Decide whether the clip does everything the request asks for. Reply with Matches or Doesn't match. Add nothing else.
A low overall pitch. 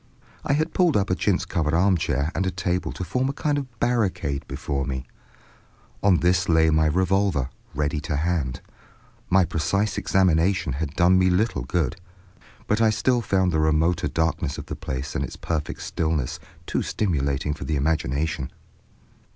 Matches